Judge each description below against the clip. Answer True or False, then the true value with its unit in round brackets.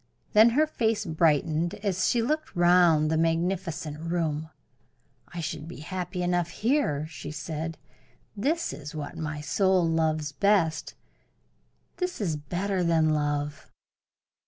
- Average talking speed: False (130 wpm)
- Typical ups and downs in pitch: True (3.5 semitones)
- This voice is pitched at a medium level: True (165 Hz)